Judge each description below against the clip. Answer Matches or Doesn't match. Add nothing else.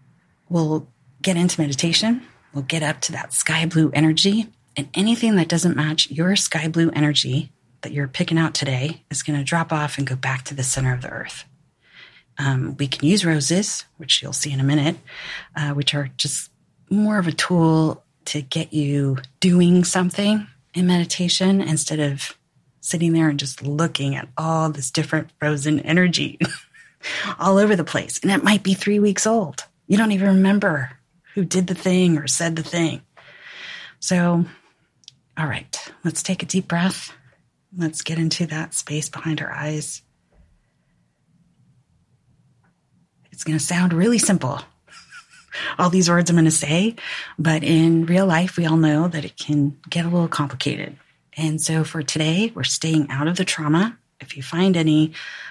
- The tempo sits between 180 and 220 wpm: Doesn't match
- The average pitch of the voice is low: Doesn't match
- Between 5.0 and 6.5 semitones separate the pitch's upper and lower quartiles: Doesn't match